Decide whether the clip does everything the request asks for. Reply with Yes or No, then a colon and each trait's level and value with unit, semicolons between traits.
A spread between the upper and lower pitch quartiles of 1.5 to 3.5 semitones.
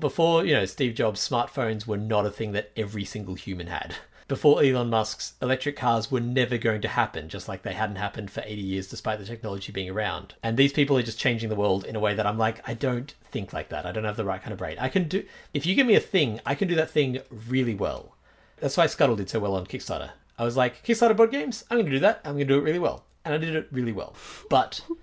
No: average, 5.2 semitones